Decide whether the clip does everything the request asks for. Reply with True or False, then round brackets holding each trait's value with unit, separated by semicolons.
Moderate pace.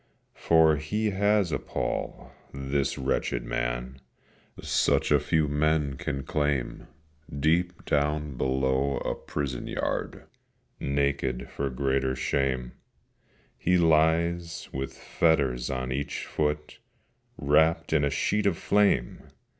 False (115 wpm)